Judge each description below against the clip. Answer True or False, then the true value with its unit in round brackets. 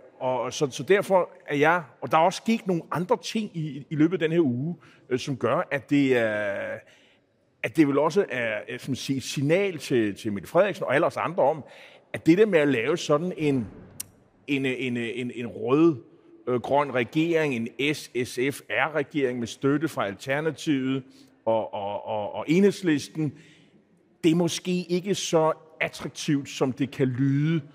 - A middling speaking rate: True (175 wpm)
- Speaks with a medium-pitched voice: True (150 Hz)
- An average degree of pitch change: True (4.1 semitones)